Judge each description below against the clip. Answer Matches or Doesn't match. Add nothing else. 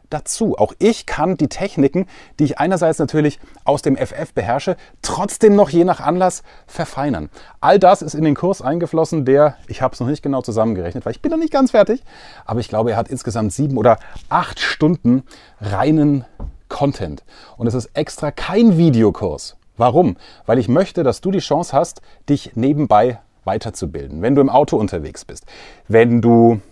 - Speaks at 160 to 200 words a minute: Matches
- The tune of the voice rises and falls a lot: Matches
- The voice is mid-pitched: Matches